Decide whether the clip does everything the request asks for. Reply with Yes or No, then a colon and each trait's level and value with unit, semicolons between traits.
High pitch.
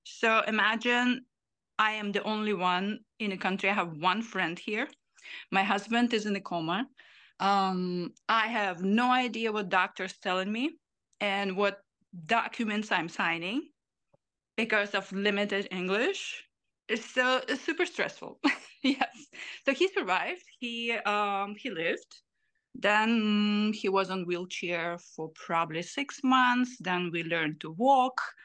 Yes: high, 210 Hz